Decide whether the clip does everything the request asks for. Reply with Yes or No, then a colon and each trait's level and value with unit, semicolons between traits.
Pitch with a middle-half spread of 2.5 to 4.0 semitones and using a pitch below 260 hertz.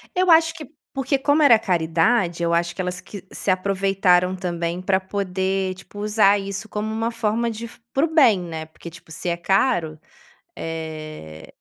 No: average, 4.5 semitones; high, 190 Hz